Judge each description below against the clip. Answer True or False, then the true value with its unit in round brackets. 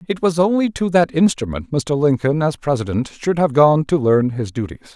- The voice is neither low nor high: True (145 Hz)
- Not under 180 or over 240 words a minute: True (205 wpm)